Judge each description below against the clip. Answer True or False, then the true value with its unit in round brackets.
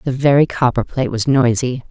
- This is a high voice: False (130 Hz)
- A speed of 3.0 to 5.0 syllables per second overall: False (5.7 syllables/s)